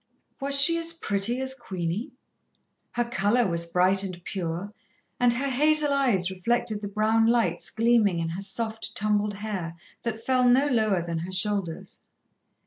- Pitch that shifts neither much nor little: Yes, average, 4.6 semitones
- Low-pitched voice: No, high, 215 Hz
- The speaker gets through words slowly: No, average, 155 wpm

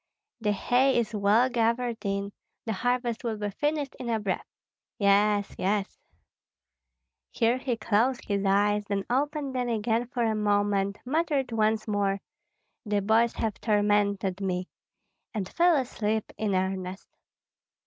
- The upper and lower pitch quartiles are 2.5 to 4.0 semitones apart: Yes, average, 3.3 semitones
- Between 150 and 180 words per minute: No, average, 140 wpm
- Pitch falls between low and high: No, high, 215 Hz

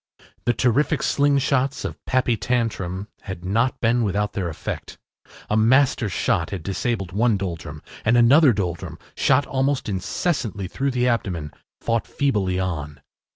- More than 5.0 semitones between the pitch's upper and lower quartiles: Yes, wide, 5.5 semitones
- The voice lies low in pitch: Yes, low, 115 Hz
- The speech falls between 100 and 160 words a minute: Yes, average, 140 wpm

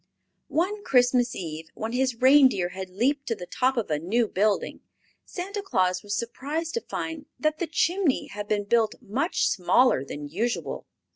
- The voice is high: Yes, high, 240 Hz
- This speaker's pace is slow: No, average, 165 wpm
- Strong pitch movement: Yes, wide, 6.9 semitones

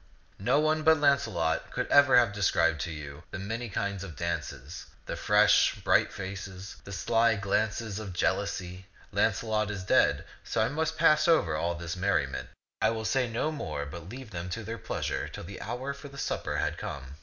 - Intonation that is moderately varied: No, wide, 6.1 semitones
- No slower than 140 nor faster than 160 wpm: No, average, 190 wpm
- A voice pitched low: Yes, low, 100 Hz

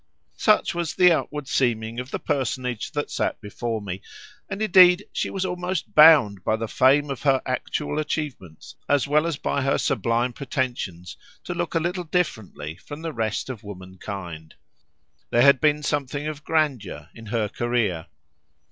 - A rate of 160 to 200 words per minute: Yes, average, 165 wpm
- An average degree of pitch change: No, wide, 5.8 semitones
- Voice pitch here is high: No, low, 130 Hz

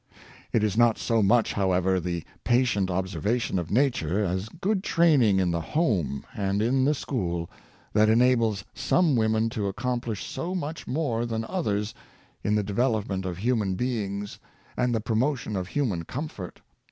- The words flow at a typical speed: Yes, average, 165 wpm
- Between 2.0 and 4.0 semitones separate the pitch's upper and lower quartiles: No, average, 4.5 semitones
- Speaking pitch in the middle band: No, low, 110 Hz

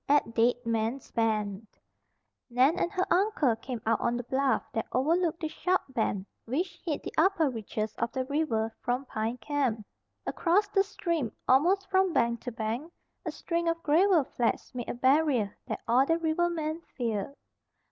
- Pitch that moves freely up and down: Yes, wide, 6.4 semitones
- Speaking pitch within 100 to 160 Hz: No, very high, 265 Hz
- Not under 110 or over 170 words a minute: Yes, average, 165 wpm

